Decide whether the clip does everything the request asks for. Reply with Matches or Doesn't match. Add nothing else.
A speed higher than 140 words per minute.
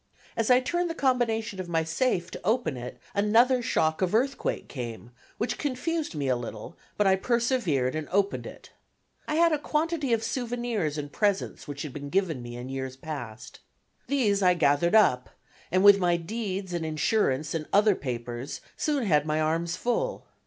Matches